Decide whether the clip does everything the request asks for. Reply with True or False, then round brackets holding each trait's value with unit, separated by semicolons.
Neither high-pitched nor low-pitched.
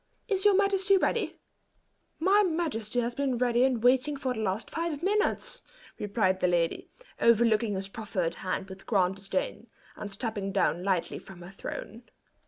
False (230 Hz)